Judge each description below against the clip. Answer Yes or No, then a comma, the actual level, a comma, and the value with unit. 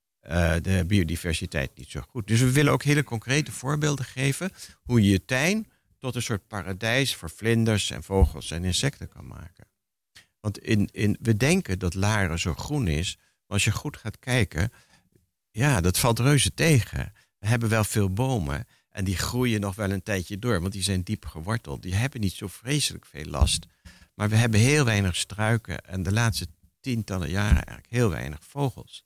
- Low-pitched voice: Yes, low, 100 Hz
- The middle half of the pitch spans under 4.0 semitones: No, average, 4.8 semitones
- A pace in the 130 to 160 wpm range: No, average, 190 wpm